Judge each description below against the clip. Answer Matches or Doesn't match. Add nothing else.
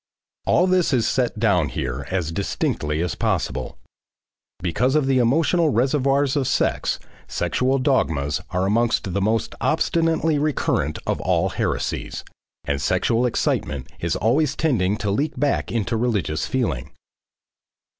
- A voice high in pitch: Doesn't match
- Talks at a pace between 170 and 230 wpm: Doesn't match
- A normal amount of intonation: Doesn't match